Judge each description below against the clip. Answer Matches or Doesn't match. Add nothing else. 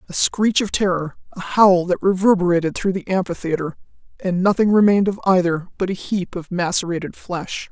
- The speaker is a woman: Matches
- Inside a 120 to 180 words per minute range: Matches